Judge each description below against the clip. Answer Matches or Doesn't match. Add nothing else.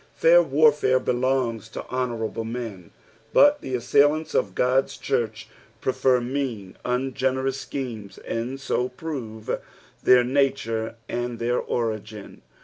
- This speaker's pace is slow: Matches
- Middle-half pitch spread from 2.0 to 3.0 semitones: Matches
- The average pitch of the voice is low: Matches